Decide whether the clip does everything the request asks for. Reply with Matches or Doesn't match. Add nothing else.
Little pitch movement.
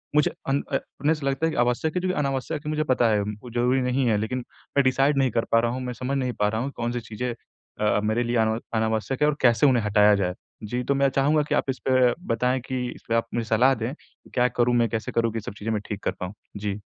Doesn't match